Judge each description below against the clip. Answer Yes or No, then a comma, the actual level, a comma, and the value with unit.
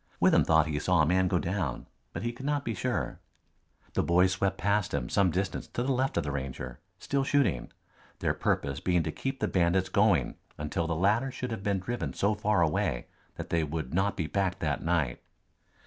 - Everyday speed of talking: No, fast, 210 wpm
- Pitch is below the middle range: Yes, very low, 90 Hz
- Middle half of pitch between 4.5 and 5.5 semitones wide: Yes, average, 4.9 semitones